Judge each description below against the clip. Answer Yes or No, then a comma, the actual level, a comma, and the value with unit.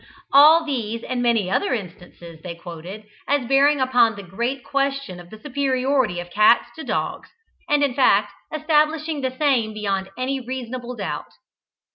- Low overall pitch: No, very high, 250 Hz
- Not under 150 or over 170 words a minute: Yes, average, 155 wpm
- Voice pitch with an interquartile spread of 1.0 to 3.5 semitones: No, average, 5.2 semitones